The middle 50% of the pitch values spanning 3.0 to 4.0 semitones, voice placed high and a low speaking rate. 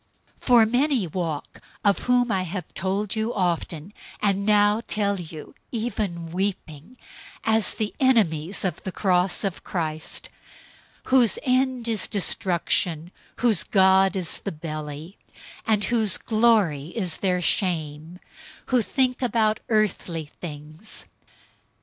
No: average, 4.6 semitones; high, 195 Hz; slow, 125 wpm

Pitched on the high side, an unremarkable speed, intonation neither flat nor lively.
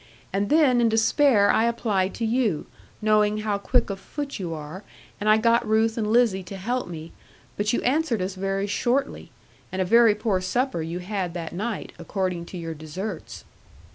Yes: high, 210 Hz; average, 185 wpm; average, 3.8 semitones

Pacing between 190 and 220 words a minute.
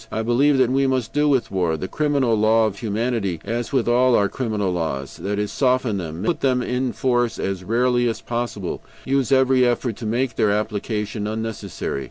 Yes: average, 195 wpm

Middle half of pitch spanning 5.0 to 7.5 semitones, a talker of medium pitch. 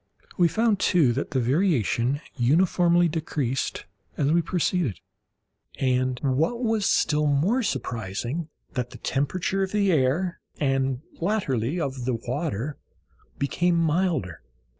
Yes: wide, 5.4 semitones; medium, 150 Hz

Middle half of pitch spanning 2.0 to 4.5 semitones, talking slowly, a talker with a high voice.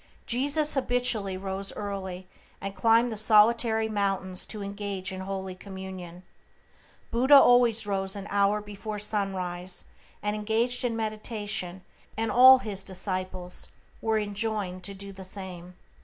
Yes: average, 2.8 semitones; slow, 130 wpm; high, 200 Hz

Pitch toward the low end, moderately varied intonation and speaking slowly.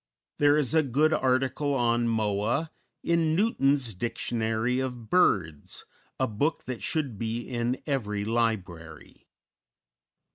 Yes: low, 120 Hz; average, 4.4 semitones; slow, 115 wpm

